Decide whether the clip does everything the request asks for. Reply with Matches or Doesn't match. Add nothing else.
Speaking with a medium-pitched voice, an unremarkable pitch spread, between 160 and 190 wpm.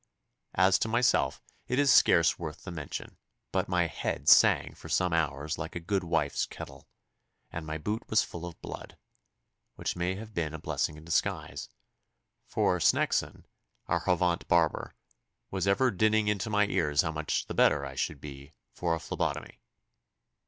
Doesn't match